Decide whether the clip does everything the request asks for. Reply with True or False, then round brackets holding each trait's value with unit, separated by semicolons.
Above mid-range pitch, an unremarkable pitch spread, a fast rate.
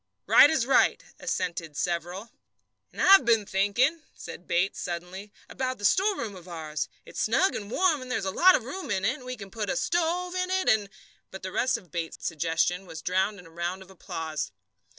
False (200 Hz; 6.8 semitones; 210 wpm)